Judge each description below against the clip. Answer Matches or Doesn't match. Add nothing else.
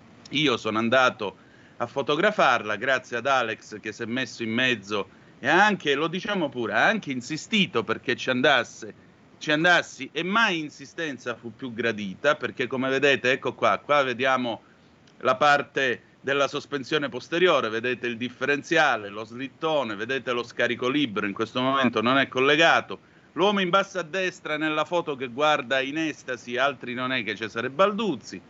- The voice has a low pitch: Matches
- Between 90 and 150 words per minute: Doesn't match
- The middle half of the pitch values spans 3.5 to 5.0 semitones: Matches